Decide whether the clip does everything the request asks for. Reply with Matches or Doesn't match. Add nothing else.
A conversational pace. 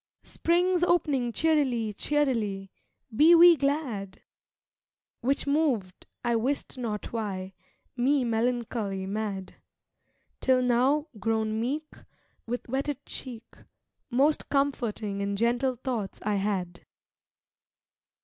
Doesn't match